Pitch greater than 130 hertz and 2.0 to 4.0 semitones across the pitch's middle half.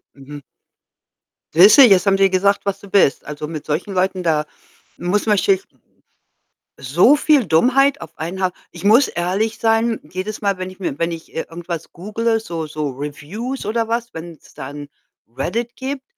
No: high, 190 Hz; wide, 5.5 semitones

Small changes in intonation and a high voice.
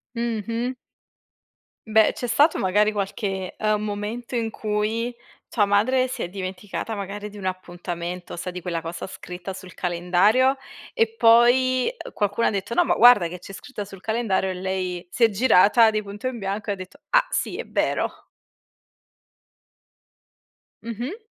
No: average, 3.9 semitones; high, 205 Hz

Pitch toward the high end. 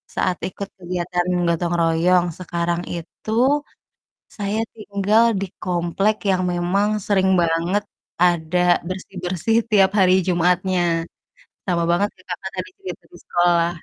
No: medium, 180 Hz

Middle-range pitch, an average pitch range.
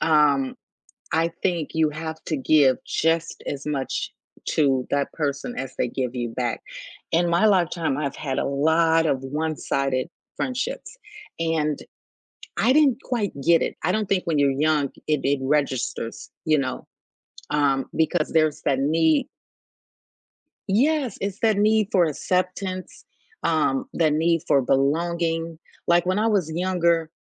Yes: medium, 160 Hz; average, 3.8 semitones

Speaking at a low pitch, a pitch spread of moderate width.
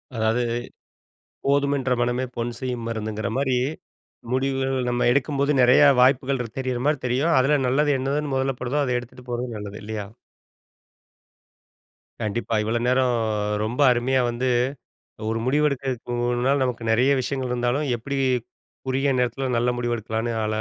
No: low, 125 Hz; narrow, 2.2 semitones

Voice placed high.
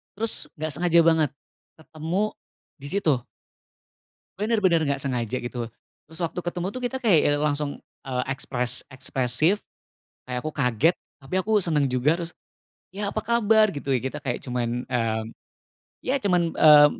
No: medium, 150 Hz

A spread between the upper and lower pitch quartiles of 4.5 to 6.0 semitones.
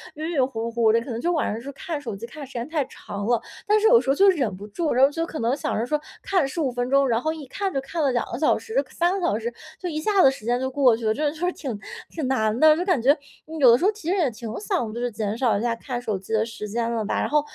Yes: wide, 5.6 semitones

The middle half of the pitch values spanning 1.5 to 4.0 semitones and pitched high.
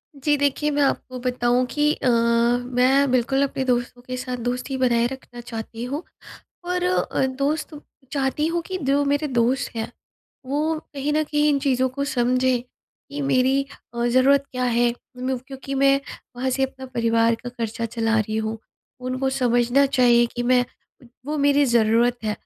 Yes: narrow, 2.4 semitones; very high, 255 Hz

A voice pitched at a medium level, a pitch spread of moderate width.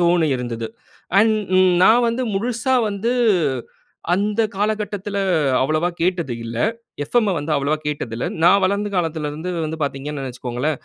No: medium, 170 Hz; wide, 6.3 semitones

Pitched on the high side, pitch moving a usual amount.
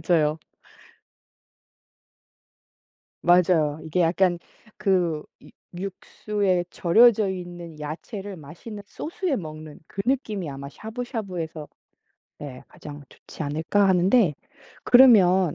No: medium, 180 Hz; average, 4.6 semitones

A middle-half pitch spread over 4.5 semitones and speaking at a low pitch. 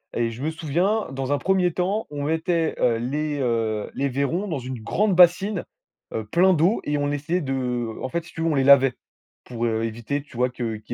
No: wide, 5.6 semitones; medium, 145 Hz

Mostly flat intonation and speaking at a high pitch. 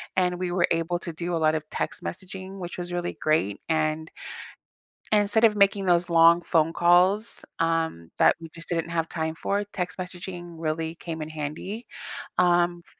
No: narrow, 2.1 semitones; medium, 175 Hz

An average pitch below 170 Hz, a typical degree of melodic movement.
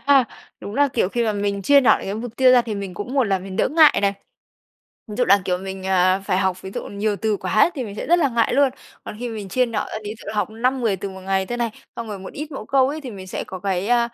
No: high, 215 Hz; average, 4.3 semitones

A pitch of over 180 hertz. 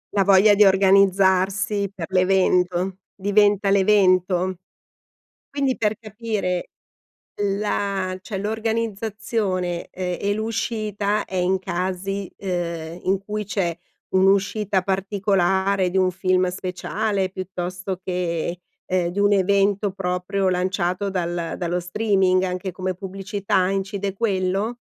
Yes: high, 190 Hz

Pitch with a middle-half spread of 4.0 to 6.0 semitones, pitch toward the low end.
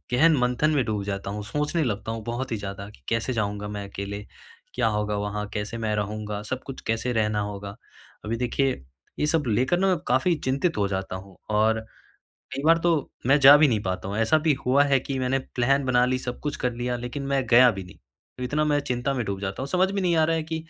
Yes: average, 5.0 semitones; low, 125 Hz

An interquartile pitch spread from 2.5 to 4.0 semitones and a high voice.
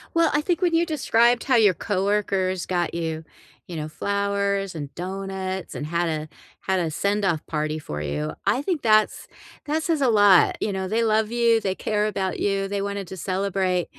Yes: average, 3.7 semitones; high, 195 Hz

